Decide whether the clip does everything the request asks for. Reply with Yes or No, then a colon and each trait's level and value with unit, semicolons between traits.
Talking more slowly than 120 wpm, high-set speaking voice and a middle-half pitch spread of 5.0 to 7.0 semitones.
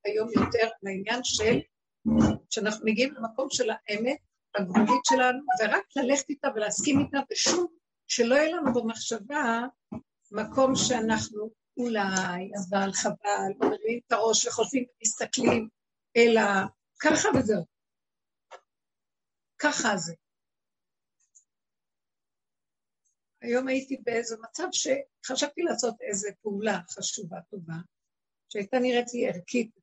No: average, 105 wpm; high, 230 Hz; average, 3.8 semitones